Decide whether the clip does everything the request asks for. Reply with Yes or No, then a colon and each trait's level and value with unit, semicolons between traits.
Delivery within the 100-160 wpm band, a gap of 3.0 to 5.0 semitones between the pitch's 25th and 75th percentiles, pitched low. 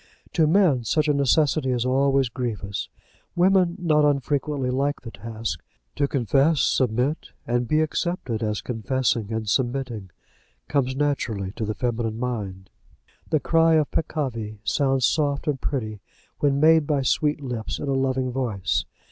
Yes: average, 150 wpm; average, 4.3 semitones; low, 130 Hz